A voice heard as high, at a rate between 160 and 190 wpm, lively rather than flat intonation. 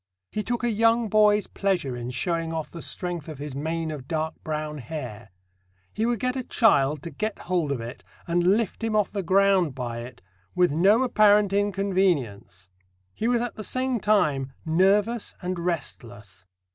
No: medium, 175 Hz; average, 175 wpm; wide, 6.6 semitones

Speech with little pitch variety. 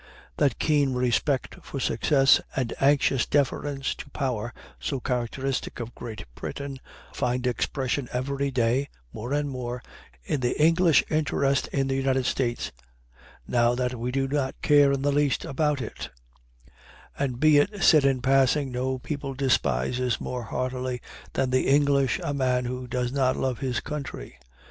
Yes: narrow, 2.0 semitones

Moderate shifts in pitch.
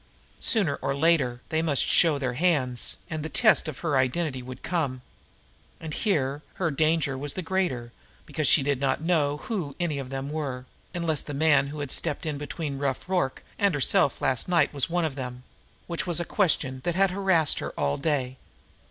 Yes: average, 3.9 semitones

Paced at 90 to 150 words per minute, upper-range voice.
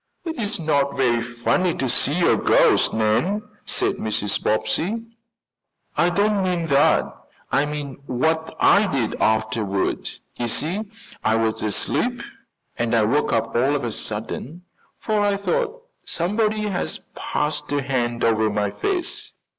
No: average, 140 wpm; medium, 140 Hz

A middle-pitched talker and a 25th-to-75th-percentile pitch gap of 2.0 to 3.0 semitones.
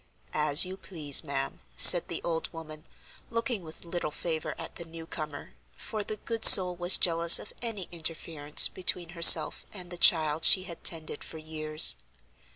Yes: medium, 165 Hz; narrow, 2.6 semitones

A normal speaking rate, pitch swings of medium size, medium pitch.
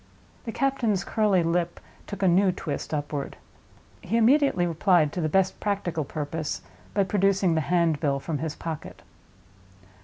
Yes: average, 145 wpm; average, 4.1 semitones; medium, 175 Hz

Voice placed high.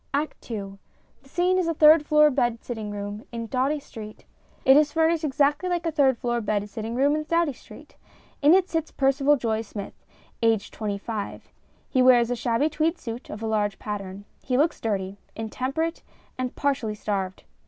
Yes: very high, 250 Hz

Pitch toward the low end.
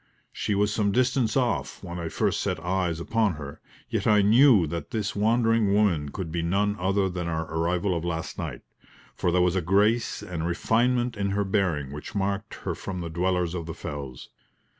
Yes: very low, 95 Hz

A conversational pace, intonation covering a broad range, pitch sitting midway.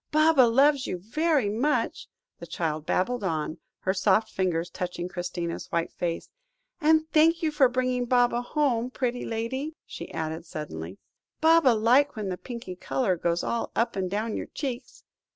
No: average, 160 wpm; wide, 7.0 semitones; high, 230 Hz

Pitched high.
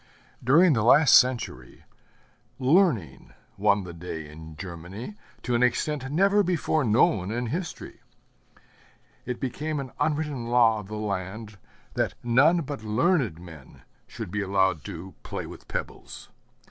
No: low, 115 Hz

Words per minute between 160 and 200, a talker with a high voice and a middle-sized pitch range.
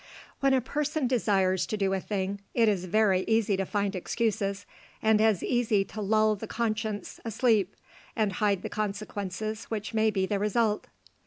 No: average, 170 wpm; high, 210 Hz; narrow, 2.0 semitones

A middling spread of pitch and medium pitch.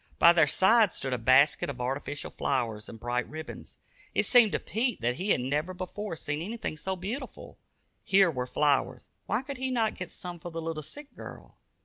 No: wide, 7.2 semitones; medium, 165 Hz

